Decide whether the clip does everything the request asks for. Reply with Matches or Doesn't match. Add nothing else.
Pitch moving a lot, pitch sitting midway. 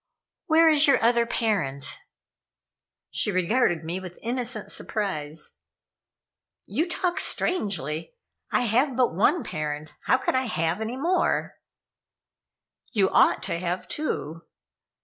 Doesn't match